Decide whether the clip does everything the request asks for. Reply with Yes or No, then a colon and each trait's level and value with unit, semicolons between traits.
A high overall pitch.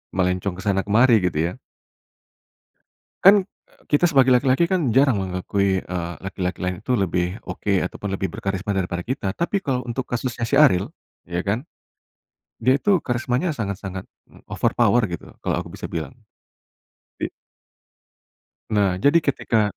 No: low, 105 Hz